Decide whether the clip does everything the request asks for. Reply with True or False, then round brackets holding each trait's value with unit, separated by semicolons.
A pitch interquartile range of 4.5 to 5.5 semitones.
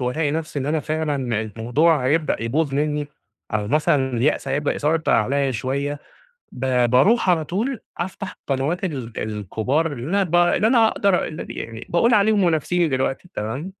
True (4.9 semitones)